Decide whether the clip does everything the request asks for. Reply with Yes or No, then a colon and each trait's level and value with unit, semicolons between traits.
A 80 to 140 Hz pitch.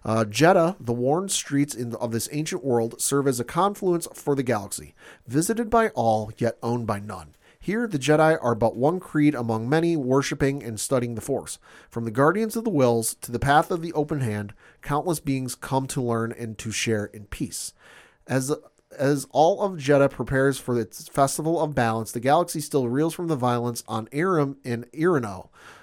Yes: low, 135 Hz